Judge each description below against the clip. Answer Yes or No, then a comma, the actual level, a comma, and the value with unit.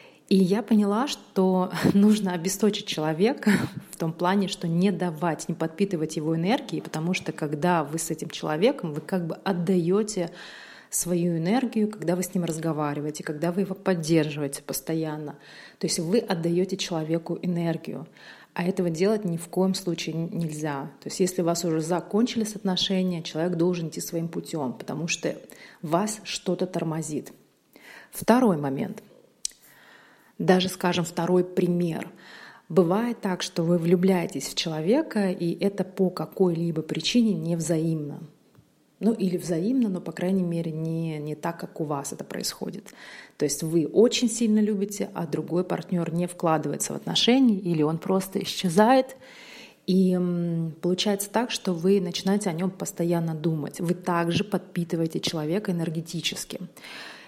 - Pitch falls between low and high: Yes, medium, 180 Hz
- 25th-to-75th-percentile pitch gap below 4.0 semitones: Yes, average, 2.8 semitones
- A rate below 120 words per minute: No, average, 145 wpm